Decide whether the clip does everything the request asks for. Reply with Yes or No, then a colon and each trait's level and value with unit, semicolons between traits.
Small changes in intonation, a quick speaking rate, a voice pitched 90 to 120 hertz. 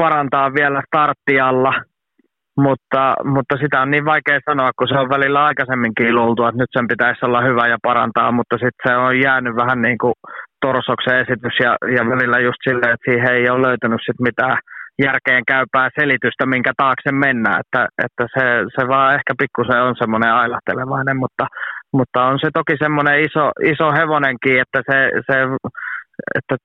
No: narrow, 2.0 semitones; fast, 170 wpm; low, 130 Hz